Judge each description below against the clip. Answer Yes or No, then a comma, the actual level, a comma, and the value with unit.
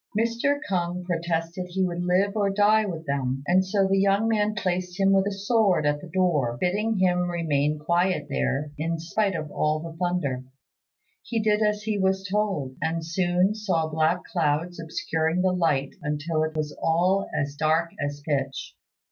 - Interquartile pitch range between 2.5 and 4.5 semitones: Yes, average, 3.8 semitones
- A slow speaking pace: No, average, 175 wpm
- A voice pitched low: No, medium, 175 Hz